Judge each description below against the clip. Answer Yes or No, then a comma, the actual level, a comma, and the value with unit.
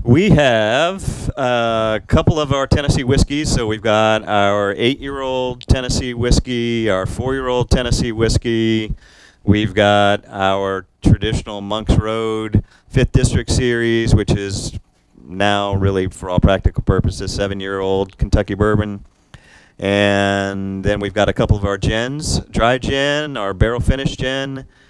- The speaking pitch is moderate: No, low, 110 Hz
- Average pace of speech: No, slow, 130 wpm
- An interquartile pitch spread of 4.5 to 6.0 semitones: No, average, 3.7 semitones